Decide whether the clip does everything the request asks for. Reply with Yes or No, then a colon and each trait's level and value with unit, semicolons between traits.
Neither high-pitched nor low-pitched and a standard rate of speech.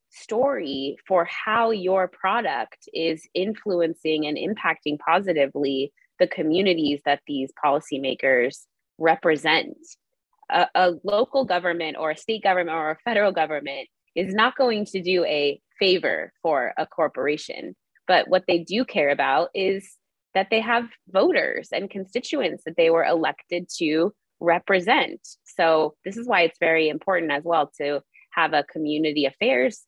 Yes: medium, 175 Hz; average, 145 wpm